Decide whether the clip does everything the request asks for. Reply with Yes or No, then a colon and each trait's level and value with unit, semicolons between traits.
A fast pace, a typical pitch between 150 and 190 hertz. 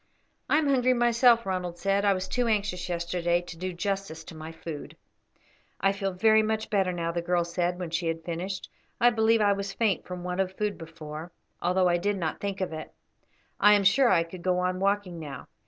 Yes: fast, 215 wpm; medium, 185 Hz